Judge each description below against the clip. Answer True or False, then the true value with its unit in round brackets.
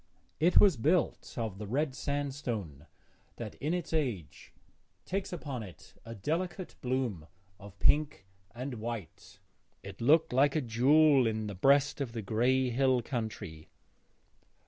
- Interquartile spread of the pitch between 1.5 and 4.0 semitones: False (5.0 semitones)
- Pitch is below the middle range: True (130 Hz)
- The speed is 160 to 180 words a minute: False (140 wpm)